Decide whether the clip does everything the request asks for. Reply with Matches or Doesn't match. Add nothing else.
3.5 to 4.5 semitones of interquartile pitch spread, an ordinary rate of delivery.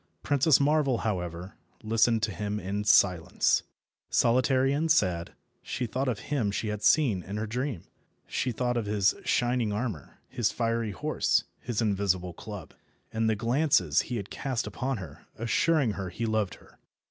Matches